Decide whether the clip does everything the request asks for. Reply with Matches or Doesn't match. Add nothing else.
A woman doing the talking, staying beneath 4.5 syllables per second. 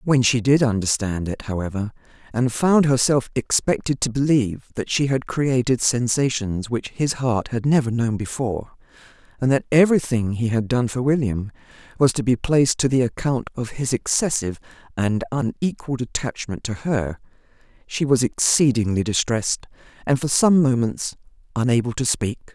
Doesn't match